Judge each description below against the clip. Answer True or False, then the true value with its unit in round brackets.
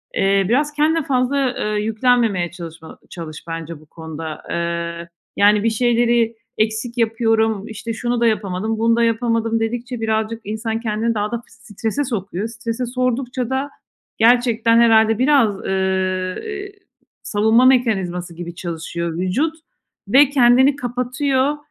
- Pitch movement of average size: True (4.1 semitones)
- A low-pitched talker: False (225 Hz)